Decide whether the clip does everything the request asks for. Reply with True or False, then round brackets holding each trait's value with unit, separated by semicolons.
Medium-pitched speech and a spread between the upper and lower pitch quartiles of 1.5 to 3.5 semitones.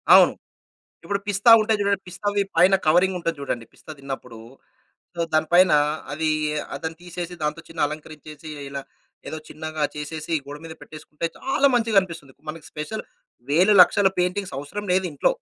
False (165 Hz; 4.2 semitones)